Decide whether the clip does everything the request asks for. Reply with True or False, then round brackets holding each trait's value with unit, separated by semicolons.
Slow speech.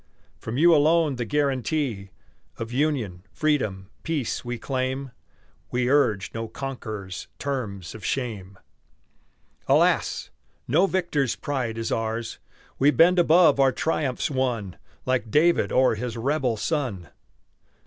True (120 wpm)